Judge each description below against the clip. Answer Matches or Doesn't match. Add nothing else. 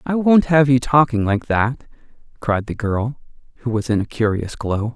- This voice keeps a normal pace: Matches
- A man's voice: Matches